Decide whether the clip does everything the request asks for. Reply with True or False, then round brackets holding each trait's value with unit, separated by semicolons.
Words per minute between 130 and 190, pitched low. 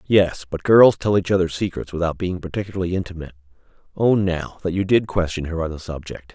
False (200 wpm; 90 Hz)